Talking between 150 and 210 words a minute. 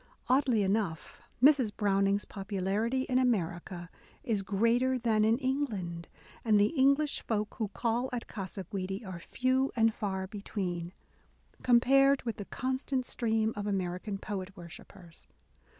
No: slow, 135 wpm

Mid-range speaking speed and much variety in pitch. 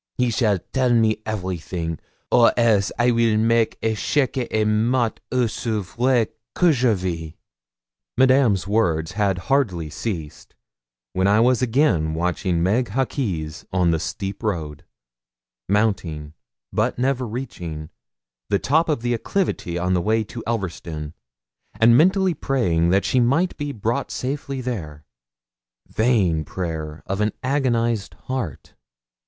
No: slow, 130 wpm; wide, 5.9 semitones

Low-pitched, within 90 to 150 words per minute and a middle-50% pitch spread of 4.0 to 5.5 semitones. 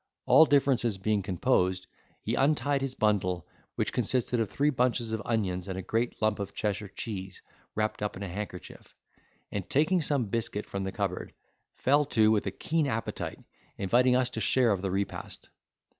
No: low, 110 Hz; average, 175 wpm; average, 4.6 semitones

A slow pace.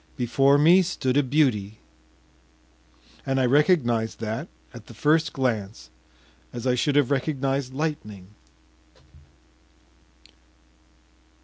Yes: slow, 100 wpm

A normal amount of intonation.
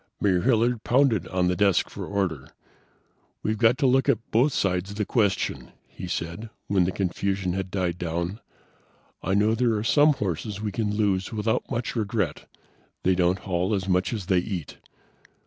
Yes: average, 3.4 semitones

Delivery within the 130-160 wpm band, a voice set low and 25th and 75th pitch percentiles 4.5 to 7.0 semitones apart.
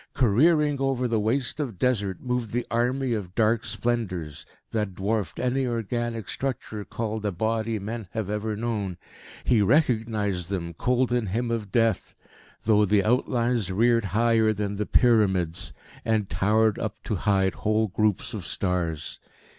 No: average, 150 wpm; low, 110 Hz; average, 2.9 semitones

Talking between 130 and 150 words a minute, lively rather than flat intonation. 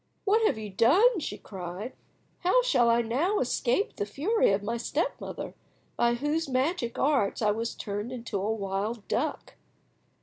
No: average, 165 wpm; wide, 6.6 semitones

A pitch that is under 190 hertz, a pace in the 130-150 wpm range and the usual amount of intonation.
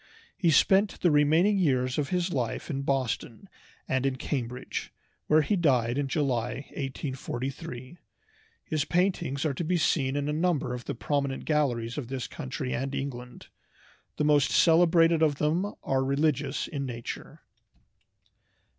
Yes: medium, 140 Hz; average, 145 wpm; average, 3.6 semitones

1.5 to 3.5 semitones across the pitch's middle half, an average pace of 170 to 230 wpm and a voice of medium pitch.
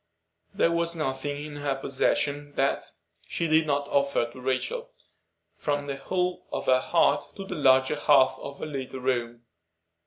No: average, 2.8 semitones; average, 155 wpm; medium, 145 Hz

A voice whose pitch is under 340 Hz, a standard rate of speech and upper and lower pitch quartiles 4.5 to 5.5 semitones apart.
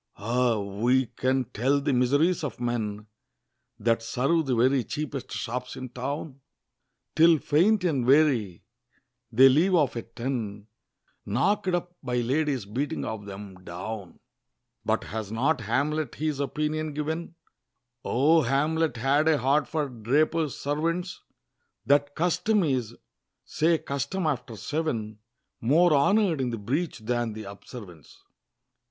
No: low, 135 Hz; slow, 130 wpm; average, 5.0 semitones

